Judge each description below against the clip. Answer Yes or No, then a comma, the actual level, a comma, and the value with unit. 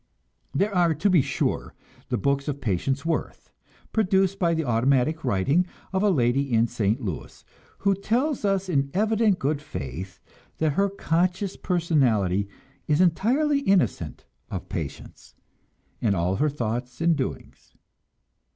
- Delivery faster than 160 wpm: No, average, 140 wpm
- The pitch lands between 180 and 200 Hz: No, medium, 155 Hz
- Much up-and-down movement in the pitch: Yes, wide, 7.8 semitones